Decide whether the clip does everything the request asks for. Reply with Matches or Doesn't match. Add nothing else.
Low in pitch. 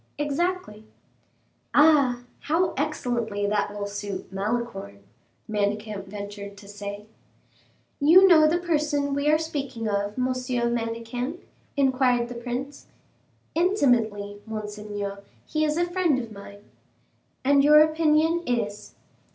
Doesn't match